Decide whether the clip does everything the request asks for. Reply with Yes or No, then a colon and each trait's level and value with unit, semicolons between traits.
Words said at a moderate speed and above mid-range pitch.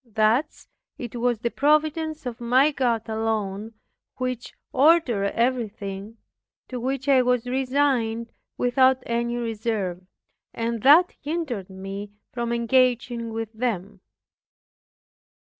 No: slow, 110 wpm; high, 235 Hz